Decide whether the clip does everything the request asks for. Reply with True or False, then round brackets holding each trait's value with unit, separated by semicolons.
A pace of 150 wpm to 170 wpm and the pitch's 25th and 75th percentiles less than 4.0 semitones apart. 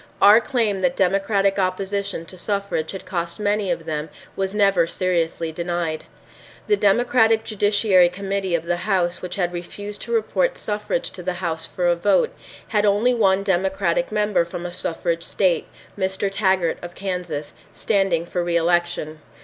True (155 wpm; 2.9 semitones)